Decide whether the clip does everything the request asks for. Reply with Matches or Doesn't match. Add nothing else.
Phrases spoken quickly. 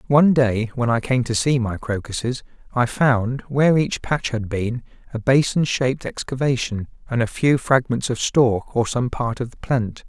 Doesn't match